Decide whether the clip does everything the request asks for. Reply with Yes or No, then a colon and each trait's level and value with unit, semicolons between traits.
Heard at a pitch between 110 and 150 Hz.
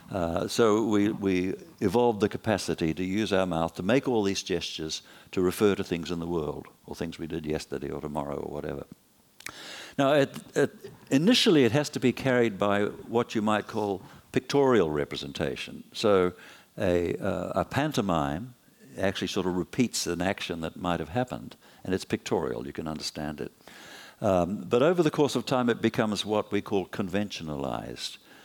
No: low, 100 Hz